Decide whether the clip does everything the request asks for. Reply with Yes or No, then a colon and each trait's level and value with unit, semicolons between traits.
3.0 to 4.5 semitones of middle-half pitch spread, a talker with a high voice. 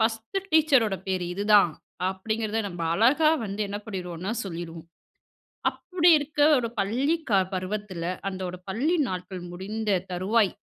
Yes: average, 3.8 semitones; high, 205 Hz